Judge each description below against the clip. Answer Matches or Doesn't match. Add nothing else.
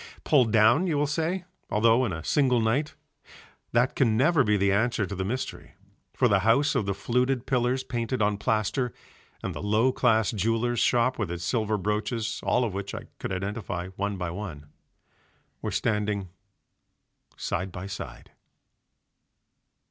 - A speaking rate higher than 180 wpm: Doesn't match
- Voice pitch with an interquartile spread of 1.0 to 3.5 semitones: Doesn't match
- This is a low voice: Matches